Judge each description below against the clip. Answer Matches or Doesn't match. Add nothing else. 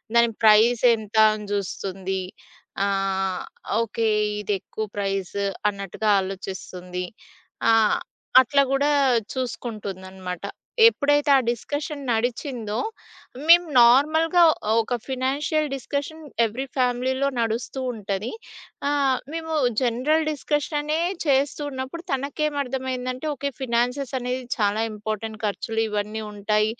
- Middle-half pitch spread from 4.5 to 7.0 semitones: Matches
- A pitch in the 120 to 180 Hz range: Doesn't match